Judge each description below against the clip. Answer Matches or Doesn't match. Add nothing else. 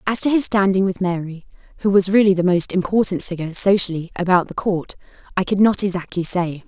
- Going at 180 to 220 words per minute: Matches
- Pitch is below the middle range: Doesn't match